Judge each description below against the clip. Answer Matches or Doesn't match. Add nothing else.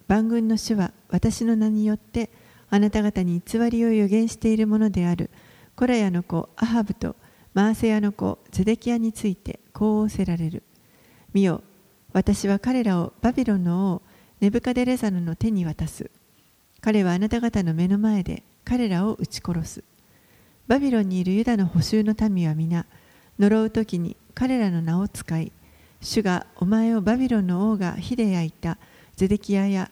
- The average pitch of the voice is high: Matches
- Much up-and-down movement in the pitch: Doesn't match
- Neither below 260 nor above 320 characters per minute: Matches